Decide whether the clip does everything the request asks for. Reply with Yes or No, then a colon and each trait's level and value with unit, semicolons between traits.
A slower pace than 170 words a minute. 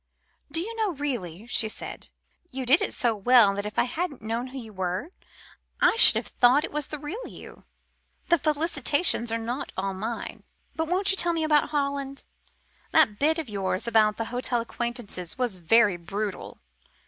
No: average, 185 wpm